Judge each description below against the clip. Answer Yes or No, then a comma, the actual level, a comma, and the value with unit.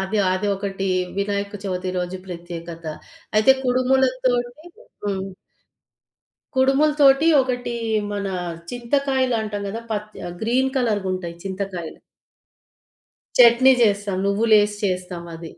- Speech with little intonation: No, average, 4.8 semitones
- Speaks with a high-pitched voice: Yes, high, 205 Hz